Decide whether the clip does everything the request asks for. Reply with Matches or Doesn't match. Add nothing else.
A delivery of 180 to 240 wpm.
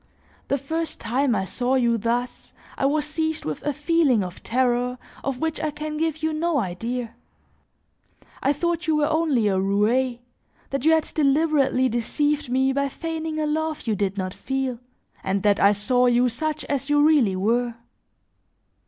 Doesn't match